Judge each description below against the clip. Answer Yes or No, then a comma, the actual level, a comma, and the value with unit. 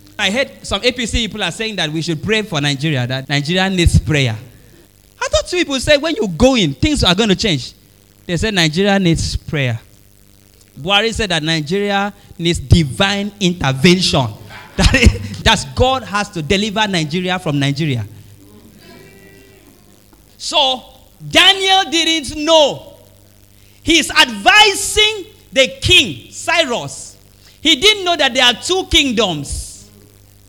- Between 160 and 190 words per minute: No, slow, 135 wpm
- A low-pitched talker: No, medium, 175 Hz